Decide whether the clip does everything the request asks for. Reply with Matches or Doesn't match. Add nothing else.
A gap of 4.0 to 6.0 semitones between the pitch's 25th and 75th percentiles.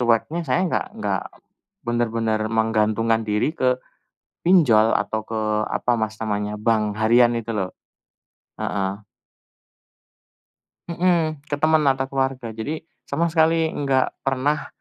Matches